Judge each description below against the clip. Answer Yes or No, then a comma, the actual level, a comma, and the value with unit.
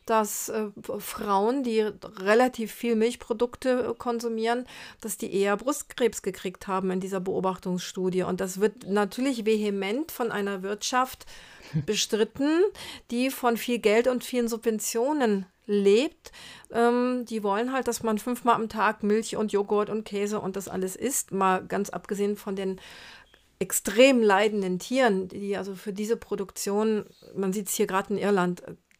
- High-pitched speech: Yes, high, 215 Hz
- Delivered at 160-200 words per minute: No, average, 150 wpm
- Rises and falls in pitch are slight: No, average, 3.2 semitones